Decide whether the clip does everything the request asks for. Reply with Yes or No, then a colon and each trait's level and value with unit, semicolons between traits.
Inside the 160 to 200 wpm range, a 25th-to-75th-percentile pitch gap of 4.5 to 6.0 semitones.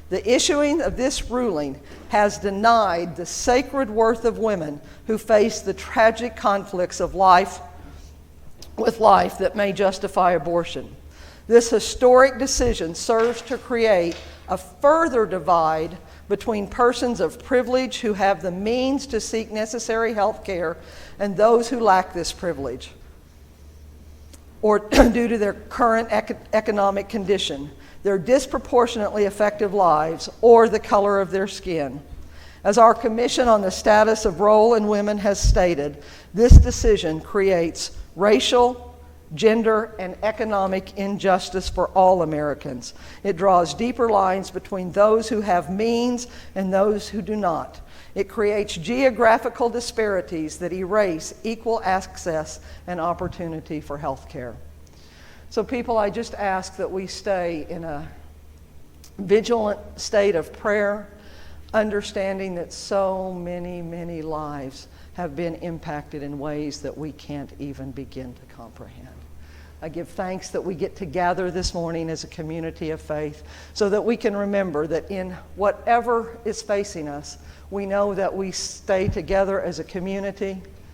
No: average, 140 wpm; average, 5.1 semitones